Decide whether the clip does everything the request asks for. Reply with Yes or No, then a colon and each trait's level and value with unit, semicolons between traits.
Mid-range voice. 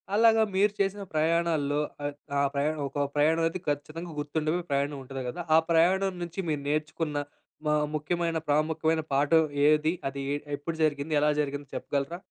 Yes: medium, 155 Hz